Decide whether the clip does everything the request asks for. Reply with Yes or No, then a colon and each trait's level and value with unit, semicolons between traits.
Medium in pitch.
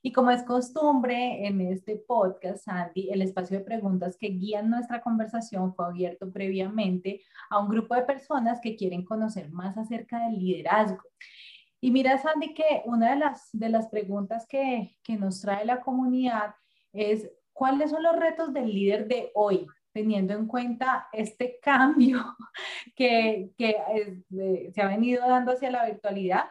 No: high, 220 Hz